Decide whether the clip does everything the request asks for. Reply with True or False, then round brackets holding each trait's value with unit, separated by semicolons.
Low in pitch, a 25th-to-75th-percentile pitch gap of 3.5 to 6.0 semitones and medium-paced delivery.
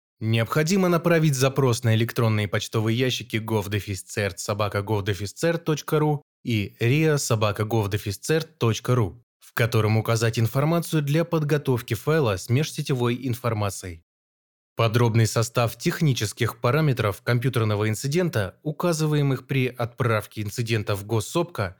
False (120 Hz; 5.3 semitones; 90 wpm)